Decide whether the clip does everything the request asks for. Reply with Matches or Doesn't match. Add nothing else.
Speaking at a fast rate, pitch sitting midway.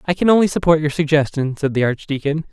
Matches